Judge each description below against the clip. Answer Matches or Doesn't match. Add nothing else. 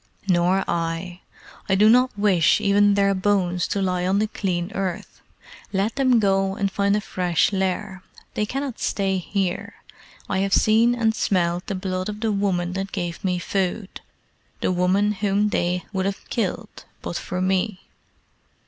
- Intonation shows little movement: Matches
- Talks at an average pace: Matches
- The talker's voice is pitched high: Matches